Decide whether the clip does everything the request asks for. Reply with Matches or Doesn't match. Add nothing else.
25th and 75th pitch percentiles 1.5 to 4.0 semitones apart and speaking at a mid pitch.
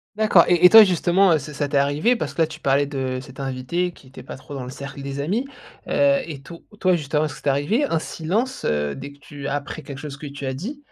Doesn't match